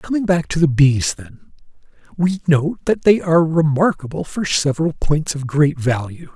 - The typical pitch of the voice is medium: Yes, medium, 155 Hz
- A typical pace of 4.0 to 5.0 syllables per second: Yes, 4.8 syllables/s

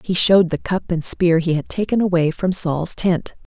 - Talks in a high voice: No, medium, 175 Hz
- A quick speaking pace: Yes, fast, 220 wpm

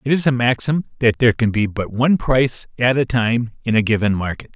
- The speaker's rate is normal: No, fast, 235 wpm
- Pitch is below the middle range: Yes, low, 120 Hz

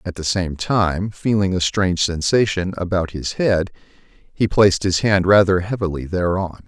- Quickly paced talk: No, average, 160 wpm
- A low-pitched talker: Yes, very low, 95 Hz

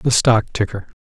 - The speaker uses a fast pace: No, average, 175 wpm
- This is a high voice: No, low, 115 Hz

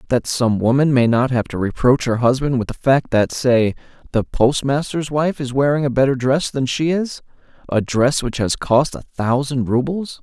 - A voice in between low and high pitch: No, low, 130 Hz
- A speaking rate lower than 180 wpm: No, average, 195 wpm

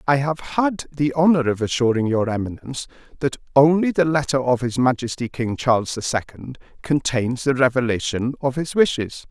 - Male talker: Yes, male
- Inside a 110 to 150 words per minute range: No, average, 170 wpm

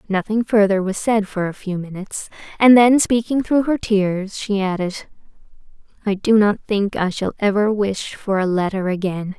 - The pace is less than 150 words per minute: No, average, 180 wpm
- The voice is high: Yes, high, 205 Hz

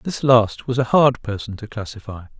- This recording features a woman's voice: No, male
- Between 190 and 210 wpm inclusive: Yes, average, 200 wpm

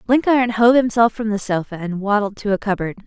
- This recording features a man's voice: No, female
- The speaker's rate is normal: No, fast, 215 wpm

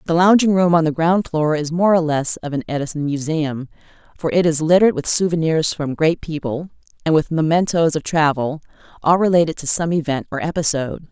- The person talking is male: No, female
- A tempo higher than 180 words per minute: Yes, average, 195 wpm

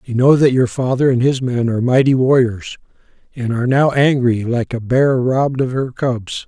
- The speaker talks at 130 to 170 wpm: No, fast, 205 wpm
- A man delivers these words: Yes, male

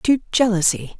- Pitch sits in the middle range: No, high, 195 Hz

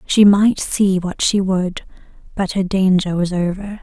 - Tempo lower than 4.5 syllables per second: Yes, 4.1 syllables/s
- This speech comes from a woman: Yes, female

